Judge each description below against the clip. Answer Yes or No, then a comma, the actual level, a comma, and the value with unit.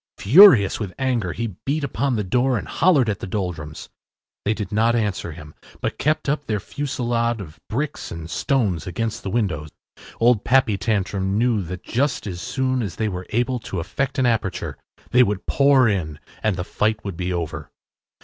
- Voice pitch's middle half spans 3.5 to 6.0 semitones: Yes, average, 5.2 semitones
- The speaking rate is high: No, average, 185 wpm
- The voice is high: No, low, 110 Hz